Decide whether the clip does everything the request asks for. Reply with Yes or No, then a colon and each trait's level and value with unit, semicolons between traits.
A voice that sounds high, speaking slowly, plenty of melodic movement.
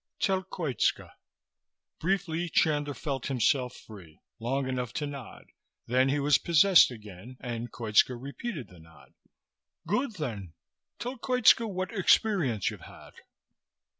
No: medium, 140 Hz; slow, 125 wpm; wide, 7.3 semitones